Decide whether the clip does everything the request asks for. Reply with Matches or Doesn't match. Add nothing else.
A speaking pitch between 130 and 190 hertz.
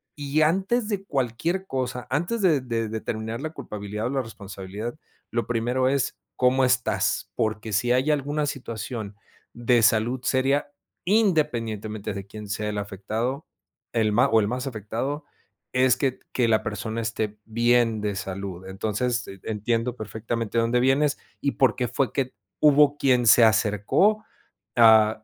Doesn't match